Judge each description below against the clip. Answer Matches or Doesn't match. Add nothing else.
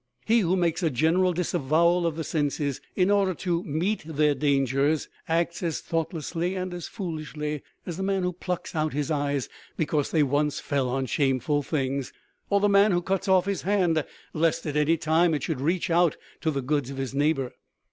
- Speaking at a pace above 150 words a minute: Matches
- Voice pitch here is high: Doesn't match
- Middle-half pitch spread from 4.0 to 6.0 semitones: Doesn't match